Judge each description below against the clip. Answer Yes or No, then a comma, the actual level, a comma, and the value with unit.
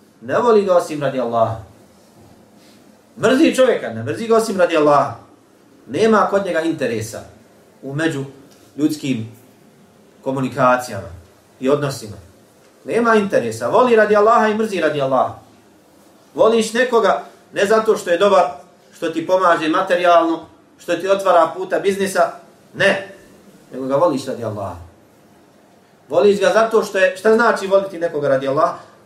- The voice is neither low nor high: Yes, medium, 170 Hz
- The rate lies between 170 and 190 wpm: No, slow, 135 wpm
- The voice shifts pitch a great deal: Yes, wide, 6.8 semitones